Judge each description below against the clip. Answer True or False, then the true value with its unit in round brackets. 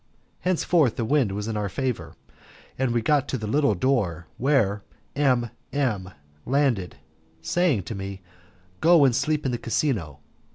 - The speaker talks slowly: False (160 wpm)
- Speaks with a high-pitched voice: False (120 Hz)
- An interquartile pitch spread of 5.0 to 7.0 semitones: True (5.6 semitones)